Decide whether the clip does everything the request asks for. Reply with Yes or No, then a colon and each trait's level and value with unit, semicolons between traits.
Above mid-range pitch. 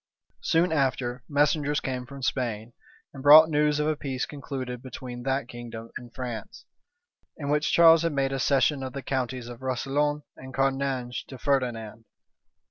No: low, 135 Hz